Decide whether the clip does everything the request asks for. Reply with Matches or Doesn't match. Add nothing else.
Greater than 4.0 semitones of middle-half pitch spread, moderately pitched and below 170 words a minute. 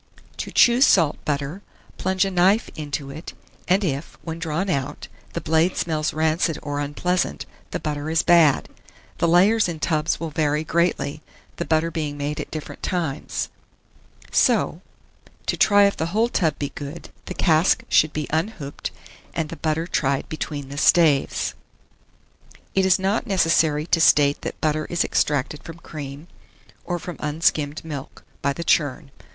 Doesn't match